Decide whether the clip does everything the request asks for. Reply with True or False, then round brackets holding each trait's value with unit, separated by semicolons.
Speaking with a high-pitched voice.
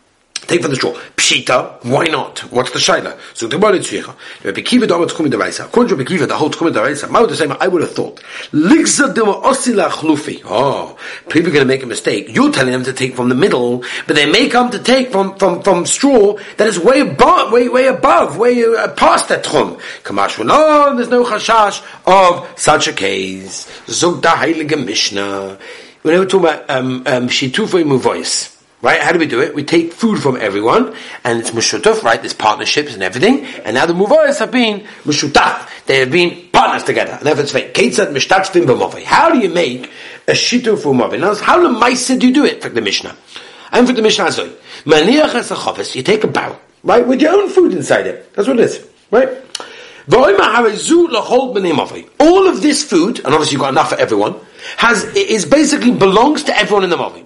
True (225 Hz)